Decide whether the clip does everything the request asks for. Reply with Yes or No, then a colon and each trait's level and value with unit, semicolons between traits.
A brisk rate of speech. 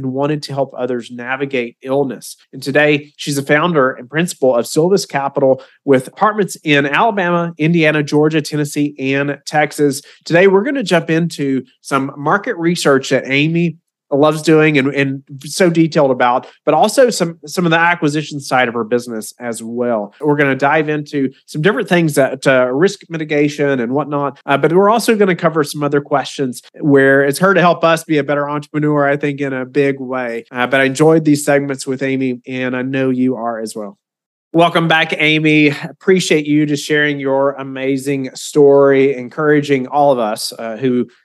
No: average, 190 wpm